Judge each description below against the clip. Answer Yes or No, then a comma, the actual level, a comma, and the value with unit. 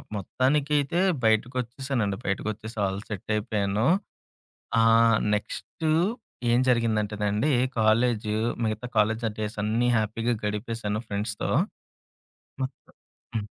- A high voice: No, low, 110 Hz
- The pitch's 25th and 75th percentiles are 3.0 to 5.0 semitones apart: No, narrow, 2.4 semitones